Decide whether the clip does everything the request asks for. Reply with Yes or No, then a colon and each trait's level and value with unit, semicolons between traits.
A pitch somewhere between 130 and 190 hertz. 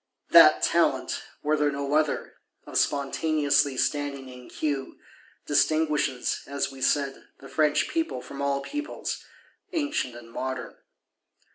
Yes: medium, 140 Hz